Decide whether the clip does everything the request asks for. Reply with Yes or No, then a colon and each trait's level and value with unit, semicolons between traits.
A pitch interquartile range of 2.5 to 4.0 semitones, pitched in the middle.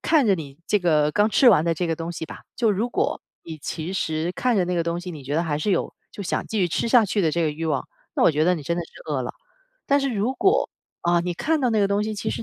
No: average, 4.9 semitones; medium, 175 Hz